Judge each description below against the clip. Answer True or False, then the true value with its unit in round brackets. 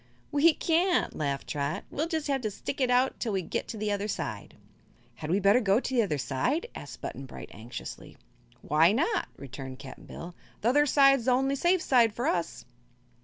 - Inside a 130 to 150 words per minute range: False (200 wpm)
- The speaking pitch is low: False (230 Hz)